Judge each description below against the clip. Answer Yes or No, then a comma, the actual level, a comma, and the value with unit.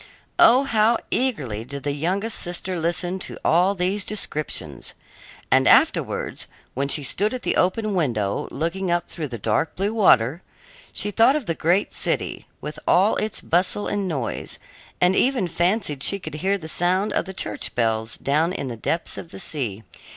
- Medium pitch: Yes, medium, 175 Hz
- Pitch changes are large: Yes, wide, 5.7 semitones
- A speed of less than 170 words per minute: No, average, 175 wpm